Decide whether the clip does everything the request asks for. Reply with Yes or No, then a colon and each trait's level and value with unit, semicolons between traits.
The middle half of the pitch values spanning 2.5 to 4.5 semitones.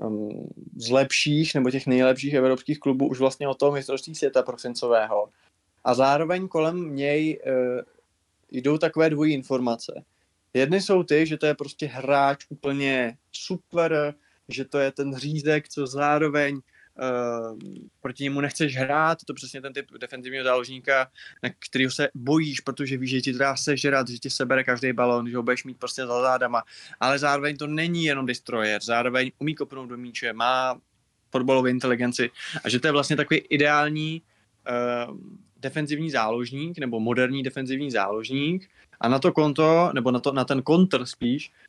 Yes: average, 2.8 semitones